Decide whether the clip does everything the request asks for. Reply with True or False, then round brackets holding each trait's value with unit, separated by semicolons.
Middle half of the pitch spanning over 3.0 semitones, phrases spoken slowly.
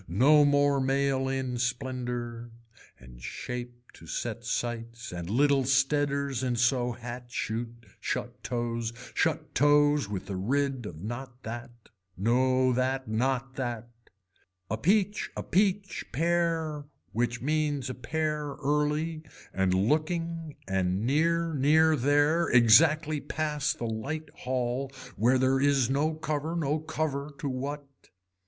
True (3.8 semitones; 130 wpm)